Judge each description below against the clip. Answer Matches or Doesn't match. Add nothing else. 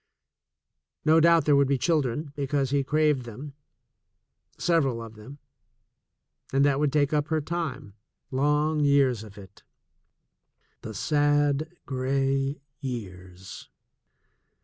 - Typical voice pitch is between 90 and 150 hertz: Matches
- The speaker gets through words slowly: Matches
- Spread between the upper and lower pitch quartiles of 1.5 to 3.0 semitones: Matches